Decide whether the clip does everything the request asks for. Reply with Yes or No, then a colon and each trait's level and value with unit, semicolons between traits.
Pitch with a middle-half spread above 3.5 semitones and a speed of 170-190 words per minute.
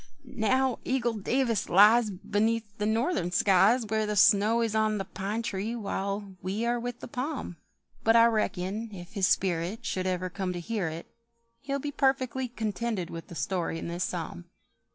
Yes: average, 3.9 semitones; average, 175 wpm